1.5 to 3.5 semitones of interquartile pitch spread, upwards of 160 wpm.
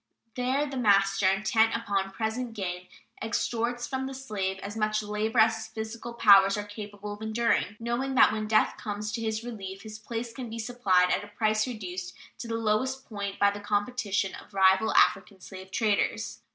Yes: narrow, 2.4 semitones; average, 185 wpm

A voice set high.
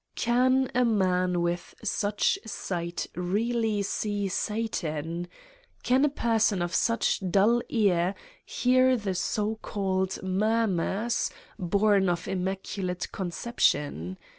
Yes: high, 200 Hz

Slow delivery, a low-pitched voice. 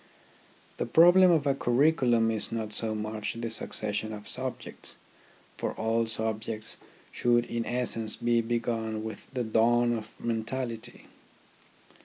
Yes: slow, 130 wpm; low, 115 Hz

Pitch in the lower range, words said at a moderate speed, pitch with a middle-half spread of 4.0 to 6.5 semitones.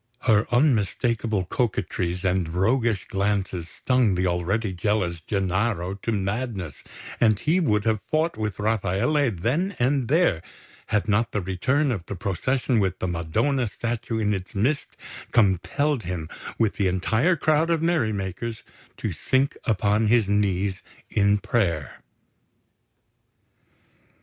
No: low, 105 Hz; slow, 130 wpm; average, 4.4 semitones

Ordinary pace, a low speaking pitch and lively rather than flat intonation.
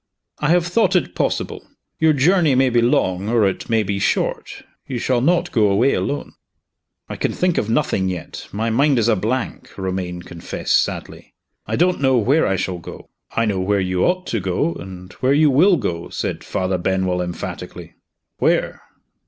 Yes: average, 185 wpm; low, 115 Hz; wide, 7.2 semitones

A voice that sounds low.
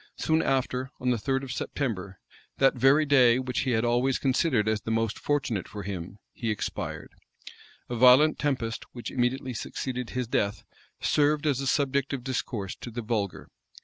Yes: low, 125 Hz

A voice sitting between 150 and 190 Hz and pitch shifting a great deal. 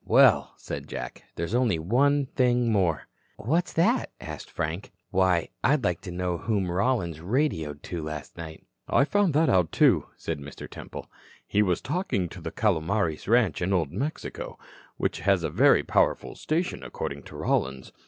No: very low, 95 Hz; wide, 7.0 semitones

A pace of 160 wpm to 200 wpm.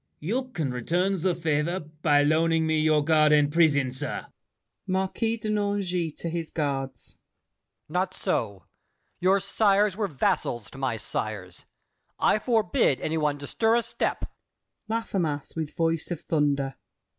No: average, 145 wpm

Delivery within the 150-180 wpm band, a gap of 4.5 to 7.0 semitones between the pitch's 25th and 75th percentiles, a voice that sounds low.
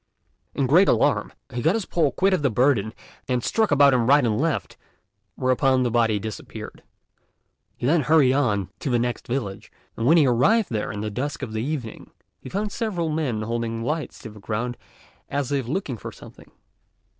No: average, 190 wpm; average, 4.9 semitones; low, 130 Hz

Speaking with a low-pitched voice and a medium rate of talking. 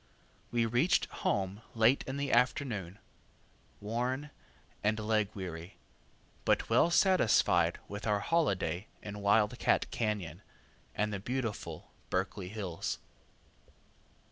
No: low, 105 Hz; slow, 110 wpm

